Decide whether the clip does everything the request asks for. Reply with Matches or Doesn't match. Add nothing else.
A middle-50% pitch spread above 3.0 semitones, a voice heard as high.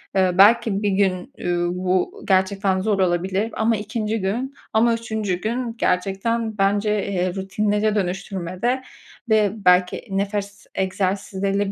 Doesn't match